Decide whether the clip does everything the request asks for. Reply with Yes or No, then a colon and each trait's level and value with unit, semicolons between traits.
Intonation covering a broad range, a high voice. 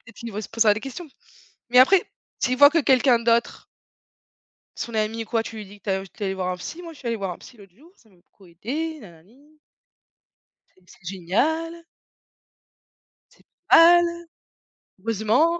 Yes: wide, 6.6 semitones; high, 230 Hz